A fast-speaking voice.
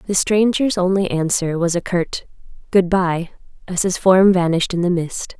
No: average, 180 wpm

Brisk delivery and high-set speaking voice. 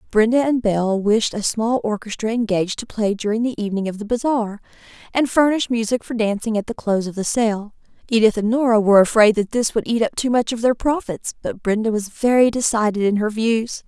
Yes: fast, 215 wpm; high, 225 Hz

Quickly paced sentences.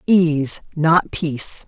No: slow, 105 wpm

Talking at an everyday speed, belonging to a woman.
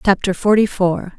Yes: average, 150 wpm; female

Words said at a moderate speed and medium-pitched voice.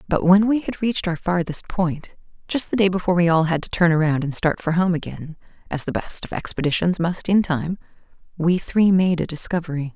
No: fast, 215 wpm; medium, 175 Hz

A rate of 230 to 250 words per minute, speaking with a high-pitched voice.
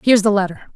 Yes: fast, 240 wpm; high, 205 Hz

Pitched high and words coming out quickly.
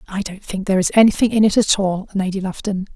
Yes: high, 195 Hz; fast, 245 wpm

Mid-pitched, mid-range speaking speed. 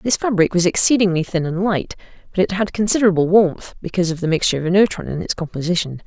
No: medium, 180 Hz; fast, 210 wpm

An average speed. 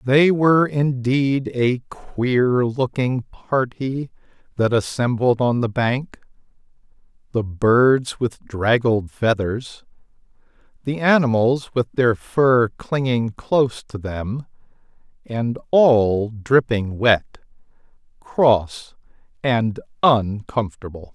No: slow, 90 wpm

